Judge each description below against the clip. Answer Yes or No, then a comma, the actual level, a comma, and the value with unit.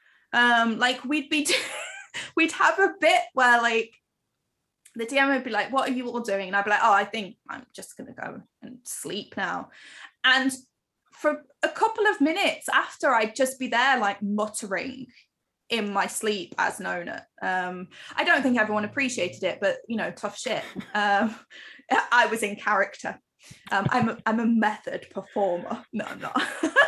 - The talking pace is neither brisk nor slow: Yes, average, 180 wpm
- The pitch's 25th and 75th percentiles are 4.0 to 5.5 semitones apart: Yes, average, 4.8 semitones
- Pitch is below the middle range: No, high, 235 Hz